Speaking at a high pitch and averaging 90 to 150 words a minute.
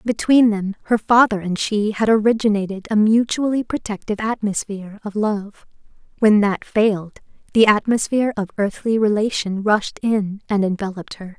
Yes: high, 210 Hz; average, 140 wpm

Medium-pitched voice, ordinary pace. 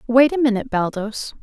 No: high, 240 Hz; average, 170 wpm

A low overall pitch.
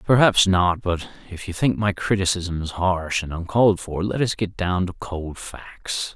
Yes: very low, 95 Hz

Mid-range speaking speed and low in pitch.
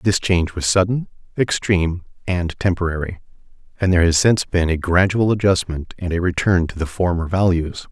Yes: average, 165 wpm; very low, 90 Hz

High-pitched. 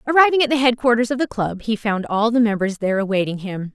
Yes: high, 225 Hz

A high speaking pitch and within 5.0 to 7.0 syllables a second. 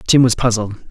No: low, 115 Hz; 5.3 syllables/s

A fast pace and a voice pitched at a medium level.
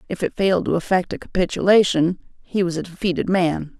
No: average, 190 wpm; medium, 180 Hz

